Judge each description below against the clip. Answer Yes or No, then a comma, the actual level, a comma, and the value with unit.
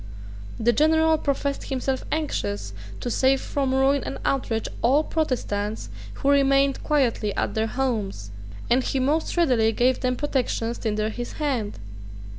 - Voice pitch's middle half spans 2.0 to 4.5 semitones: Yes, average, 3.9 semitones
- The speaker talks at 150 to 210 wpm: No, average, 140 wpm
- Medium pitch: No, very high, 260 Hz